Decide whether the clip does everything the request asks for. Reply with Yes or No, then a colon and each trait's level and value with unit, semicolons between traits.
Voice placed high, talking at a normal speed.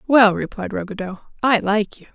Yes: high, 210 Hz; average, 170 wpm